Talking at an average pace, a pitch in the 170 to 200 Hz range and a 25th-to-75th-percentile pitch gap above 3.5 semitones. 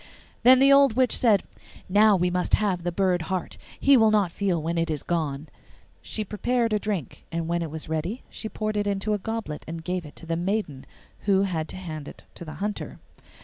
No: fast, 220 wpm; medium, 185 Hz; average, 4.4 semitones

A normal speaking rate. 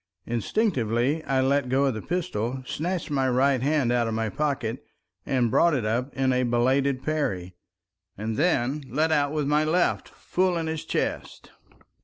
Yes: average, 170 wpm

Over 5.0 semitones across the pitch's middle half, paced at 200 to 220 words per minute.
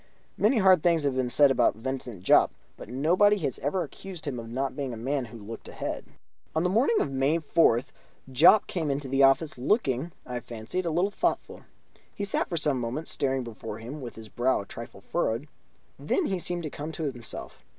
Yes: wide, 5.5 semitones; fast, 205 wpm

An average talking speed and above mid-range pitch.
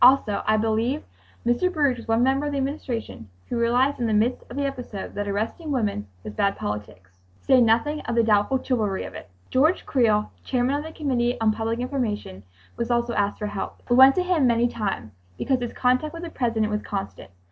No: fast, 210 wpm; high, 240 Hz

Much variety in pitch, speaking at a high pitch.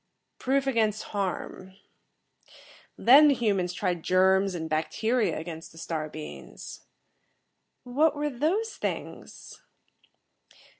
Yes: wide, 7.0 semitones; high, 200 Hz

